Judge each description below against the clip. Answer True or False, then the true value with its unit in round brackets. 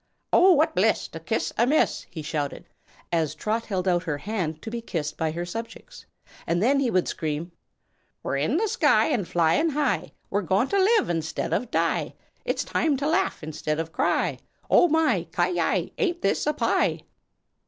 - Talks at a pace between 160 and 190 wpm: True (185 wpm)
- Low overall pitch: False (200 Hz)